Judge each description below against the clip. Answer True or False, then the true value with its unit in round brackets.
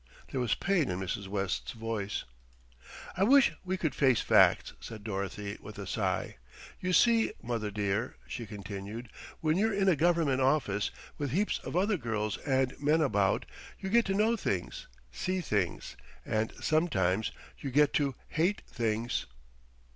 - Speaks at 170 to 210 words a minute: False (155 wpm)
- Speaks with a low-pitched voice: True (130 Hz)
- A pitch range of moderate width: False (8.9 semitones)